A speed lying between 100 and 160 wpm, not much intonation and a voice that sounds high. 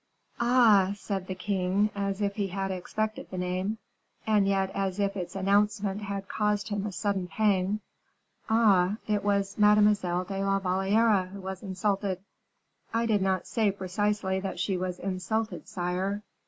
Yes: average, 155 wpm; narrow, 1.7 semitones; high, 195 Hz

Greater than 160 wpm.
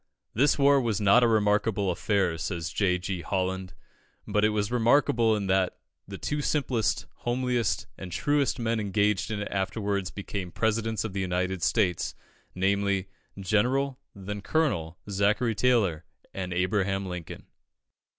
No: average, 140 wpm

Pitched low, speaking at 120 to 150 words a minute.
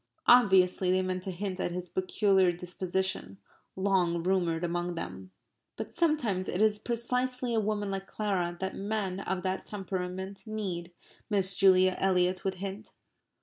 No: high, 190 Hz; average, 145 wpm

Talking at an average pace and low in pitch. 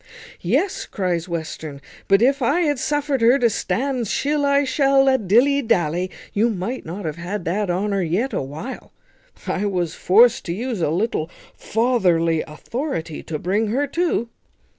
No: average, 160 wpm; high, 215 Hz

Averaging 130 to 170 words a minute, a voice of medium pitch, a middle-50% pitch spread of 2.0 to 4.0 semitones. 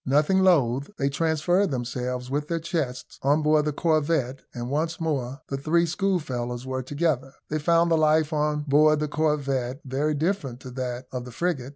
No: average, 180 wpm; medium, 150 Hz; average, 3.5 semitones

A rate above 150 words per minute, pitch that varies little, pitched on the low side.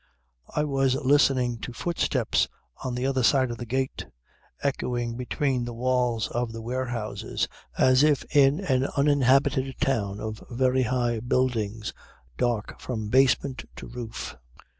No: average, 140 wpm; narrow, 2.3 semitones; low, 125 Hz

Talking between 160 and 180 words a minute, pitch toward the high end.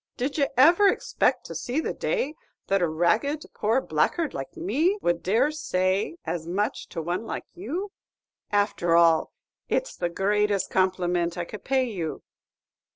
Yes: average, 165 wpm; high, 205 Hz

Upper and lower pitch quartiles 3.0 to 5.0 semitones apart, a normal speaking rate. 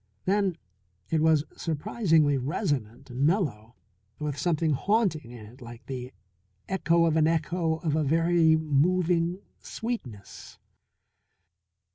No: average, 4.0 semitones; slow, 115 wpm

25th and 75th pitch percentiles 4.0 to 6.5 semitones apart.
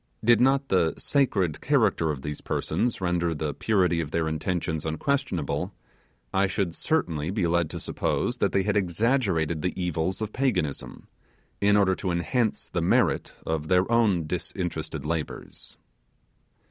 Yes: average, 4.6 semitones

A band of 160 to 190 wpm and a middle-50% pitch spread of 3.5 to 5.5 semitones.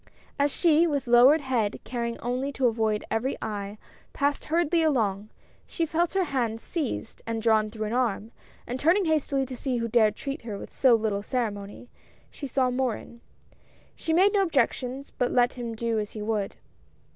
Yes: average, 180 wpm; average, 4.2 semitones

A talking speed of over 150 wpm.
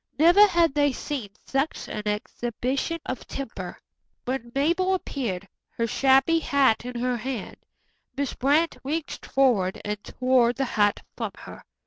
No: average, 140 wpm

